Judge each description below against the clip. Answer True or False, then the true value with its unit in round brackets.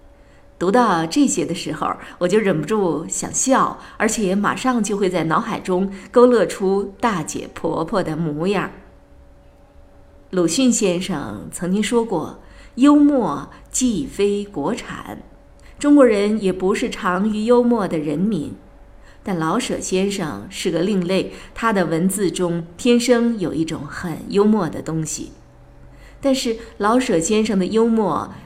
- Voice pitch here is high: True (195 Hz)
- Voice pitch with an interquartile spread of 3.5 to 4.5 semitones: False (5.4 semitones)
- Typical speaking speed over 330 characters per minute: False (200 characters per minute)